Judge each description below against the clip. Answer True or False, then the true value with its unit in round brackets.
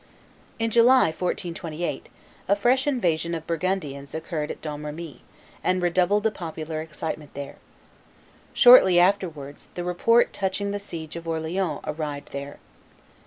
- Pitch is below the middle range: False (170 Hz)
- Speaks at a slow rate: True (125 wpm)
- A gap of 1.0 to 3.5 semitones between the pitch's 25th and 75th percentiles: False (4.0 semitones)